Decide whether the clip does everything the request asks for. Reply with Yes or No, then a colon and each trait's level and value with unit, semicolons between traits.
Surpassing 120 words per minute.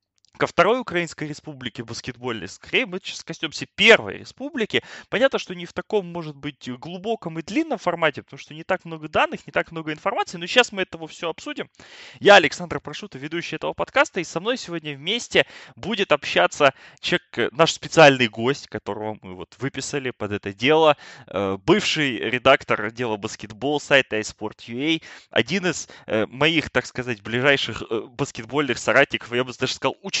Yes: fast, 160 wpm